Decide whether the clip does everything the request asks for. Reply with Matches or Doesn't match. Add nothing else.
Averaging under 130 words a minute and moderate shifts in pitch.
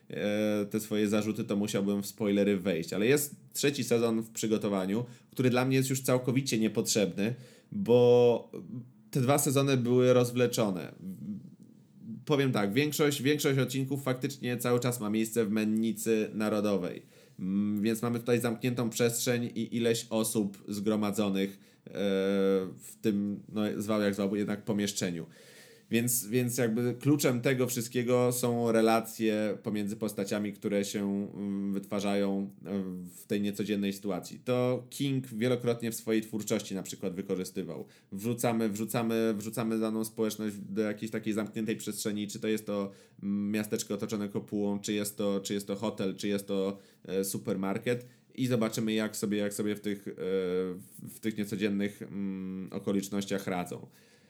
Doesn't match